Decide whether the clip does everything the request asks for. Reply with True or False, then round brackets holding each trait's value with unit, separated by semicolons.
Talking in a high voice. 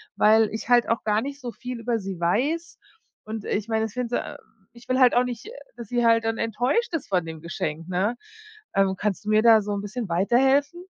True (225 Hz)